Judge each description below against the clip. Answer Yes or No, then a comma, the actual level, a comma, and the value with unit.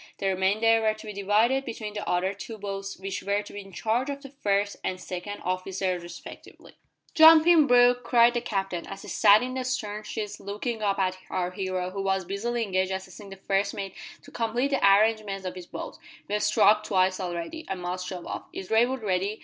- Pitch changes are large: No, average, 3.0 semitones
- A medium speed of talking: No, fast, 210 wpm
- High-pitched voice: Yes, high, 200 Hz